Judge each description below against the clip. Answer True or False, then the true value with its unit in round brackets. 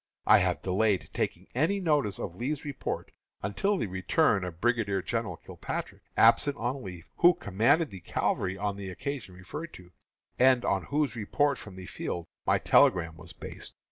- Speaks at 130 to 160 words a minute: False (170 wpm)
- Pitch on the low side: True (105 Hz)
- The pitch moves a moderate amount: False (7.2 semitones)